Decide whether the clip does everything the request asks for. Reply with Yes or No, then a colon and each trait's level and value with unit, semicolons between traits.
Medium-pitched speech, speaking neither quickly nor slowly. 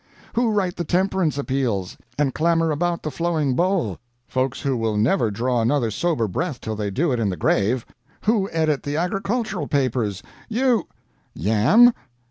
Yes: medium, 145 Hz; average, 160 wpm